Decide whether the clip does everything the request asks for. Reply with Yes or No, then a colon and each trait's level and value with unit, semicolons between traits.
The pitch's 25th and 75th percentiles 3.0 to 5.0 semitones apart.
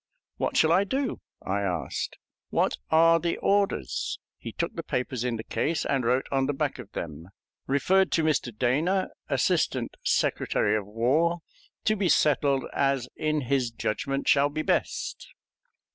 No: wide, 5.5 semitones